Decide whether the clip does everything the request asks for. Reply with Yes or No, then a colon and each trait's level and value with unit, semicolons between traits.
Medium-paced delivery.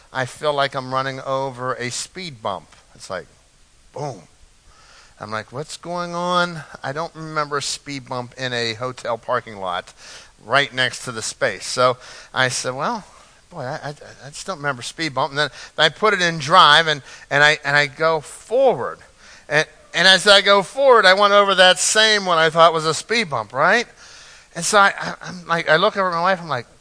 No: fast, 210 wpm